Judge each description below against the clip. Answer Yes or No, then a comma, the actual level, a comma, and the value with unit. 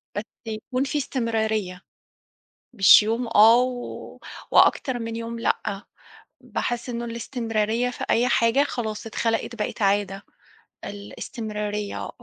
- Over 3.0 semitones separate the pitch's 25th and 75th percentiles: No, narrow, 2.4 semitones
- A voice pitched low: No, high, 230 Hz